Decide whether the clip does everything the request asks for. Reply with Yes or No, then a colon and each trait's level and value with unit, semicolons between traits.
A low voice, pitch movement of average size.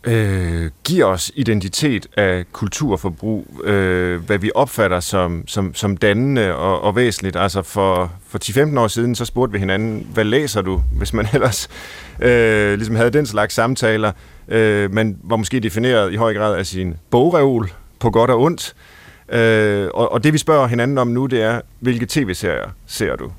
Yes: low, 105 Hz; average, 3.7 semitones